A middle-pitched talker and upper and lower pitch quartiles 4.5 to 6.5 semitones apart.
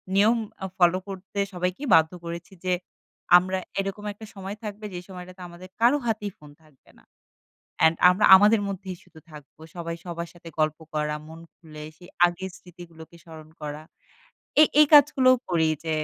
No: medium, 180 Hz; average, 3.5 semitones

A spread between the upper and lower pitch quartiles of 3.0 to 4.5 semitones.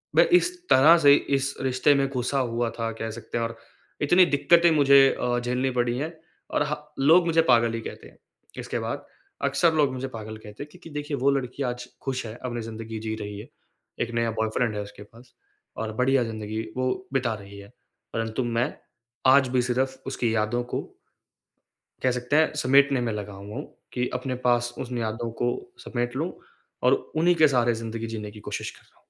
Yes: average, 3.4 semitones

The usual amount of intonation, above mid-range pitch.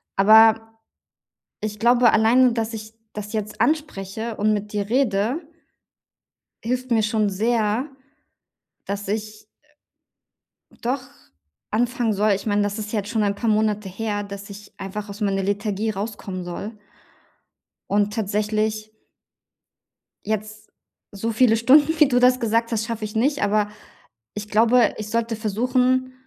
No: narrow, 2.0 semitones; high, 215 Hz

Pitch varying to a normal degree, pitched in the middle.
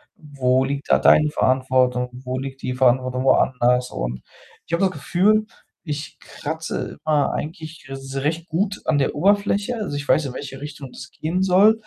Yes: average, 4.8 semitones; medium, 145 Hz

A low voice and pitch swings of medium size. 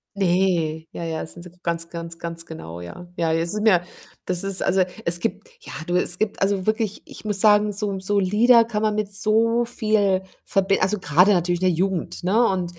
No: high, 190 Hz; average, 3.5 semitones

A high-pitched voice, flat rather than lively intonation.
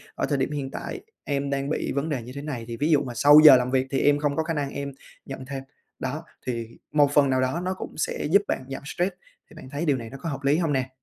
No: medium, 140 Hz; narrow, 2.1 semitones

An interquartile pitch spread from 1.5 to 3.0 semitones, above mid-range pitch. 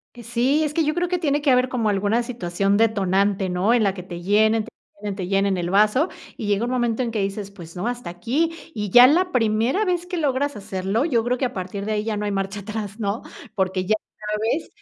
No: average, 4.2 semitones; high, 215 Hz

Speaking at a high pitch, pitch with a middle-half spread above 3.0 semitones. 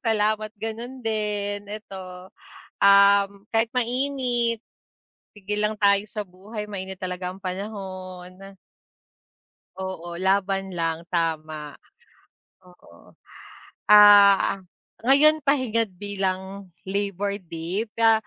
No: high, 200 Hz; narrow, 2.6 semitones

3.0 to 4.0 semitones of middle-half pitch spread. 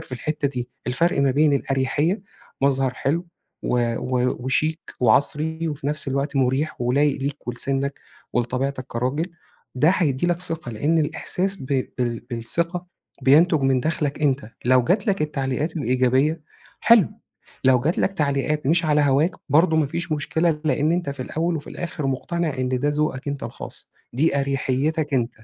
Yes: average, 3.5 semitones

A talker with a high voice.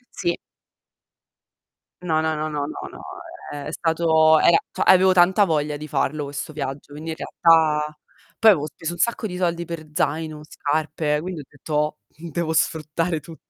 No: medium, 160 Hz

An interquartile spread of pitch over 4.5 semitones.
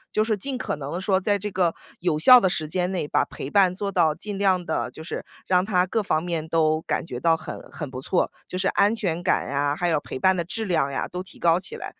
No: average, 3.6 semitones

